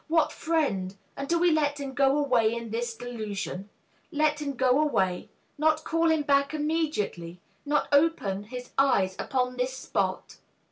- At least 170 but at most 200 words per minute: No, average, 155 wpm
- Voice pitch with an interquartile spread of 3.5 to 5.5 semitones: Yes, average, 5.2 semitones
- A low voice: No, very high, 275 Hz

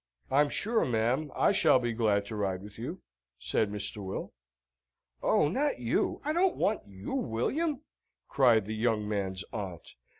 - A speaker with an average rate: Yes, average, 160 wpm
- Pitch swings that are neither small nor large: No, wide, 7.1 semitones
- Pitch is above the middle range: No, low, 115 Hz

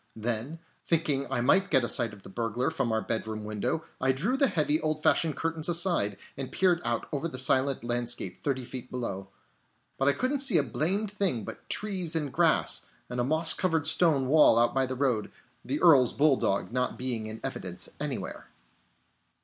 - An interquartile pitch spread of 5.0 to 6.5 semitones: Yes, wide, 5.4 semitones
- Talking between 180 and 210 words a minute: Yes, average, 190 wpm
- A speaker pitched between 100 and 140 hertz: Yes, low, 135 Hz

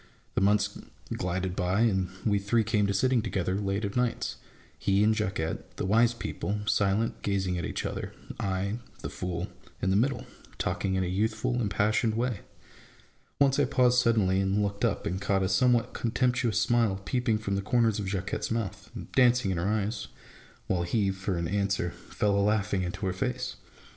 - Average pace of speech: Yes, average, 185 wpm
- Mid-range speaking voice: No, low, 100 Hz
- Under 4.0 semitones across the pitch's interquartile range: Yes, average, 3.2 semitones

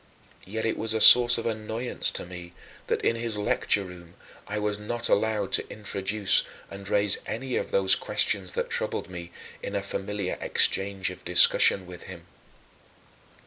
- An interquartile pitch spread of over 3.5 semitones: No, average, 2.9 semitones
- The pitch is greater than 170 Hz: No, low, 100 Hz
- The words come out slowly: No, average, 165 wpm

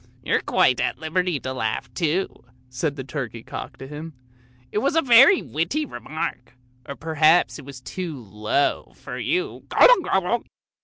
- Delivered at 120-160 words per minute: No, average, 170 wpm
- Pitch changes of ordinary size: No, wide, 6.4 semitones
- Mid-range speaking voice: Yes, medium, 155 Hz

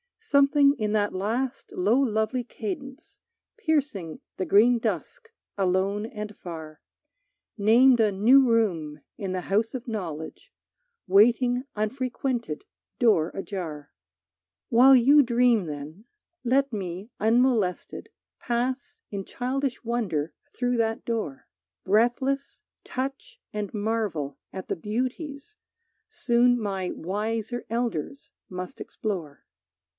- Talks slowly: Yes, slow, 110 wpm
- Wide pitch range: No, average, 4.8 semitones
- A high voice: Yes, high, 225 Hz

